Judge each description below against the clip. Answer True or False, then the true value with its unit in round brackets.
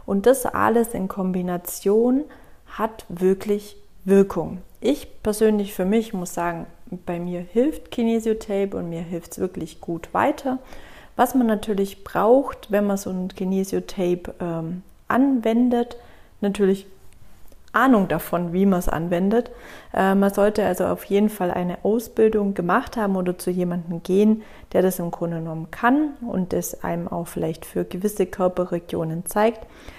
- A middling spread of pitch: True (3.7 semitones)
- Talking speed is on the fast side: False (145 wpm)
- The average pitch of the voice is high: True (195 Hz)